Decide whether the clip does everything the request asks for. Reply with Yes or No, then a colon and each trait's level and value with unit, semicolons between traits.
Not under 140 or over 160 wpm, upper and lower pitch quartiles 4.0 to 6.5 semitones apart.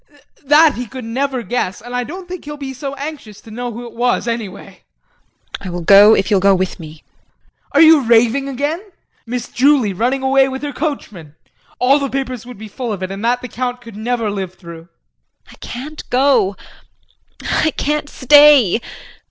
No: average, 195 wpm; average, 4.9 semitones